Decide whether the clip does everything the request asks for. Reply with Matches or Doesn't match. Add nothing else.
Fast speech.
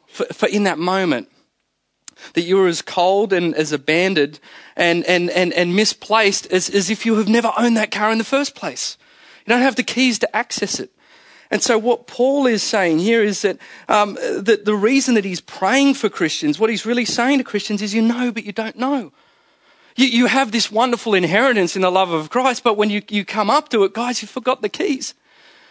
Matches